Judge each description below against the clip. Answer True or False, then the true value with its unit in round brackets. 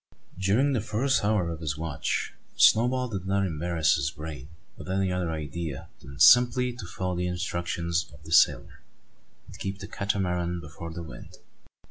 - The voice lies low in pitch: True (90 Hz)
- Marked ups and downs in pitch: False (3.6 semitones)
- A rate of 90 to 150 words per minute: False (165 wpm)